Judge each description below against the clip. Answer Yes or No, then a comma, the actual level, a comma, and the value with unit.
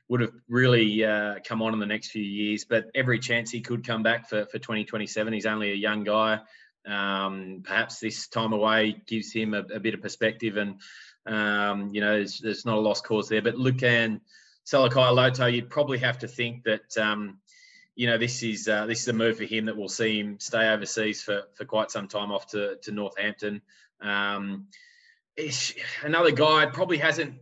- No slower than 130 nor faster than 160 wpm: No, average, 195 wpm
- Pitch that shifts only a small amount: Yes, narrow, 2.2 semitones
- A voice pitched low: Yes, low, 110 Hz